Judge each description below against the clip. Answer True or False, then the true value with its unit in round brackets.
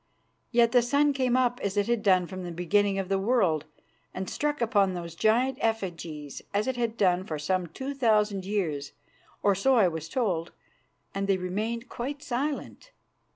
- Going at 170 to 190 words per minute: True (180 wpm)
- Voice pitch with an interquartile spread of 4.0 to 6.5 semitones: True (4.9 semitones)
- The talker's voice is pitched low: False (205 Hz)